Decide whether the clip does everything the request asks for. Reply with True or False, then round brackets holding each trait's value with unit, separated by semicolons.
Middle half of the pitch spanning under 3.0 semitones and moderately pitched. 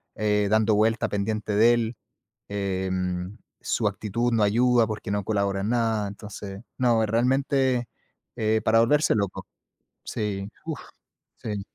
False (2.4 semitones; 110 Hz)